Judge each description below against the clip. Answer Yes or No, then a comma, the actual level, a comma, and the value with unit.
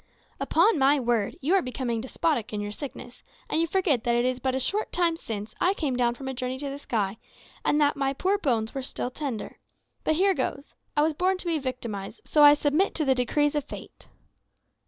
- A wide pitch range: No, average, 4.1 semitones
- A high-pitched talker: Yes, very high, 270 Hz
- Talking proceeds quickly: Yes, fast, 220 wpm